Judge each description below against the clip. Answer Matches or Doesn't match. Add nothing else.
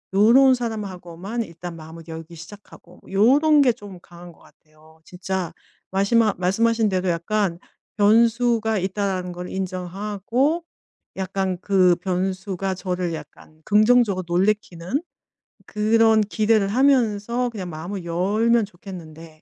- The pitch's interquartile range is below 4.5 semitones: Matches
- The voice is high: Matches